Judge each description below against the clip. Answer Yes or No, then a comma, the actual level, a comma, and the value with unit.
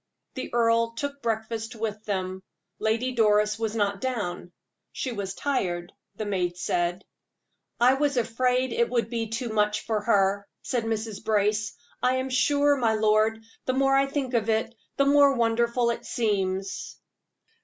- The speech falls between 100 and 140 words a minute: No, average, 155 wpm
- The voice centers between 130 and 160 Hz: No, high, 225 Hz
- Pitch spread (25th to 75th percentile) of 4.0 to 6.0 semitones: No, average, 3.1 semitones